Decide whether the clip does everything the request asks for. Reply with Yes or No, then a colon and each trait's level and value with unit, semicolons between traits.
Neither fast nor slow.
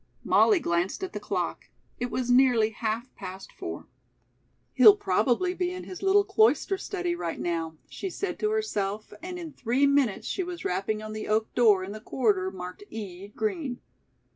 Yes: average, 175 wpm